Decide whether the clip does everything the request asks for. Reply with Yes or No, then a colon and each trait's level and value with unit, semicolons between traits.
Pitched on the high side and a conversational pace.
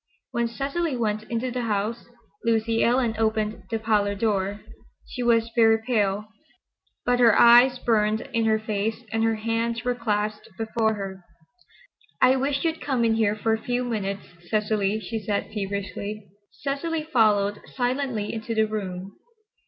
Yes: high, 225 Hz; average, 150 wpm